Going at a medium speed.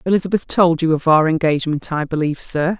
Yes: average, 195 wpm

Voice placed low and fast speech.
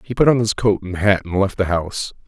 Yes: low, 100 Hz; fast, 290 wpm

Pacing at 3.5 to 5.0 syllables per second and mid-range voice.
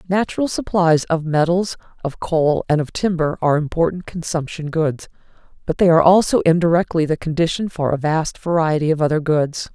No: 5.4 syllables/s; medium, 165 Hz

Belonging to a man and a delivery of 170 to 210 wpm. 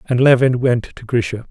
Yes: male; average, 200 wpm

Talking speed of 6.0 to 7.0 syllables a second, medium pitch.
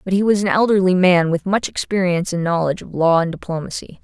Yes: 6.4 syllables/s; medium, 180 Hz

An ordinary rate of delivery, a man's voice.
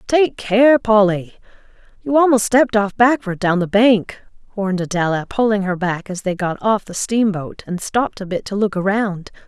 No: average, 185 wpm; female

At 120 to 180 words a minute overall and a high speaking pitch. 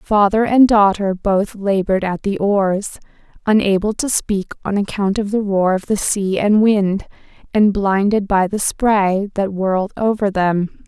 Yes: average, 165 wpm; high, 200 Hz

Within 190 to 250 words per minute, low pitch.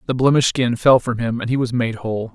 No: fast, 280 wpm; low, 120 Hz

